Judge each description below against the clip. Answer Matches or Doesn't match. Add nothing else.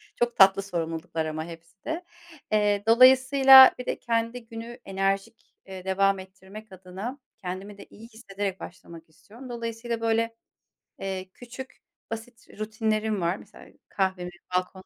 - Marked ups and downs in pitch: Doesn't match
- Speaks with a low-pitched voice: Doesn't match